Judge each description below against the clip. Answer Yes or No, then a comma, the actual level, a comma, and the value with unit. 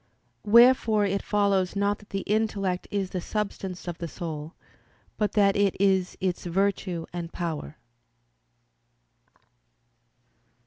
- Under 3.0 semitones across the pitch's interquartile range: Yes, narrow, 2.5 semitones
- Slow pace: Yes, slow, 120 wpm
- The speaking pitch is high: Yes, high, 195 Hz